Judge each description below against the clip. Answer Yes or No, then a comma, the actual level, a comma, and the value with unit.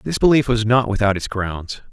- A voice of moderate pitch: No, low, 110 Hz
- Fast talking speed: Yes, fast, 220 wpm